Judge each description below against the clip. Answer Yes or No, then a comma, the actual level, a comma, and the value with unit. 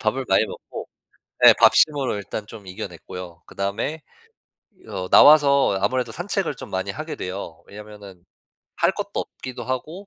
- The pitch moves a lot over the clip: Yes, wide, 6.4 semitones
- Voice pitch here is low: Yes, low, 110 Hz